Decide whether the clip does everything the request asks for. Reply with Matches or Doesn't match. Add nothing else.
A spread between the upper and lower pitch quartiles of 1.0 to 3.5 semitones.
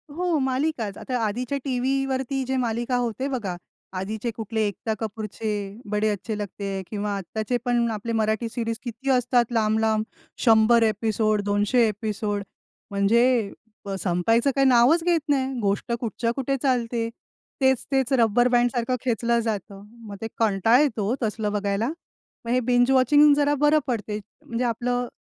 Matches